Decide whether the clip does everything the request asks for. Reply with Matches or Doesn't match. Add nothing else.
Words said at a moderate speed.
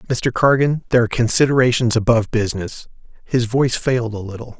Matches